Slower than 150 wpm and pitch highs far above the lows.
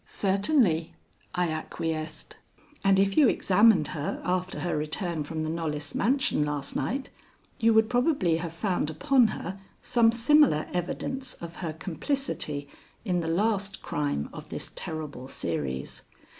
Yes: average, 140 wpm; wide, 6.1 semitones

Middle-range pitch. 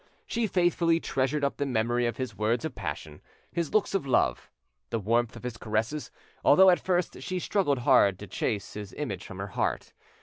No: low, 130 Hz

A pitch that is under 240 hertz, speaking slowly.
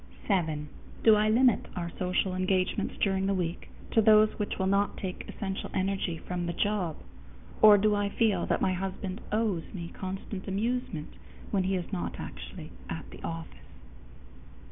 No: high, 190 Hz; average, 165 wpm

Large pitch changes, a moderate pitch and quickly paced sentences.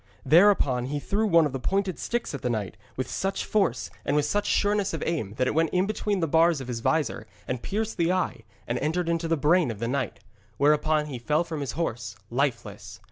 Yes: wide, 5.9 semitones; medium, 155 Hz; fast, 225 wpm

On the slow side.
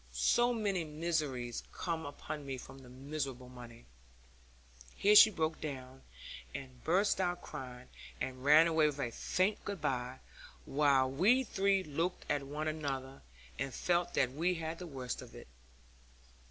No: average, 155 wpm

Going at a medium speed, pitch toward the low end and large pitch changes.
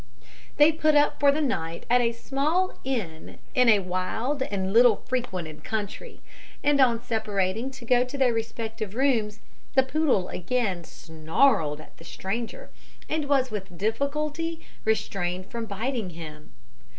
No: average, 145 wpm; high, 230 Hz; wide, 6.1 semitones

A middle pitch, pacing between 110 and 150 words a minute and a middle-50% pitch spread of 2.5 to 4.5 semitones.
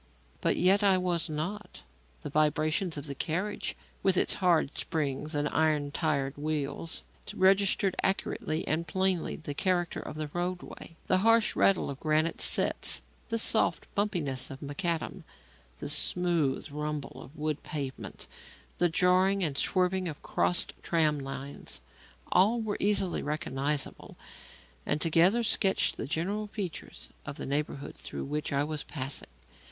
Yes: medium, 160 Hz; average, 140 wpm; average, 4.1 semitones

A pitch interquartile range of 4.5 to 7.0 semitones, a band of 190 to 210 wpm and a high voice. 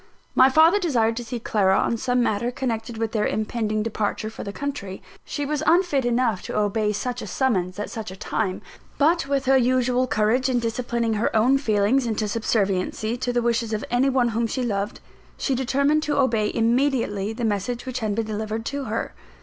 No: average, 3.2 semitones; average, 200 wpm; high, 235 Hz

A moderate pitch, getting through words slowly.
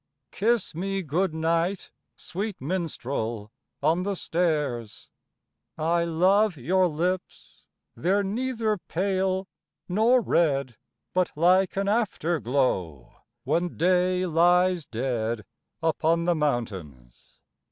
Yes: medium, 170 Hz; slow, 105 wpm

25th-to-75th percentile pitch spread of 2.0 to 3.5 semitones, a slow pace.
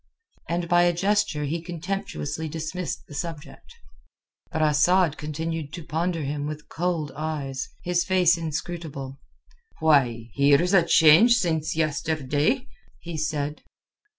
Yes: average, 2.8 semitones; slow, 125 wpm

